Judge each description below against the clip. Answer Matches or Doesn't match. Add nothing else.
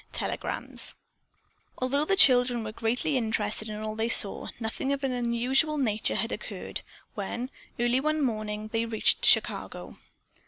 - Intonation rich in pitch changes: Doesn't match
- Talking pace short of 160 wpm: Matches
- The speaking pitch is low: Doesn't match